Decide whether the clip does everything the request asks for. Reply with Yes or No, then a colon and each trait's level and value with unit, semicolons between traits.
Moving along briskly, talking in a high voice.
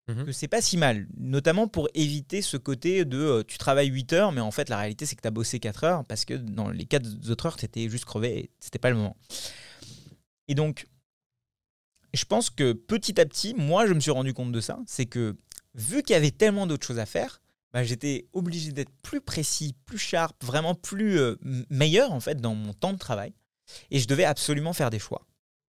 No: fast, 225 wpm; medium, 140 Hz